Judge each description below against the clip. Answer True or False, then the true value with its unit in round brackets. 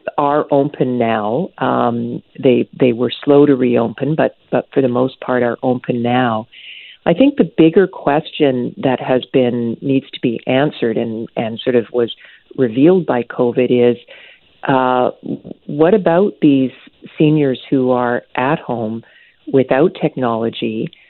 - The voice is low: True (130 Hz)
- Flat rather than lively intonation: False (3.5 semitones)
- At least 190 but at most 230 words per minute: False (145 wpm)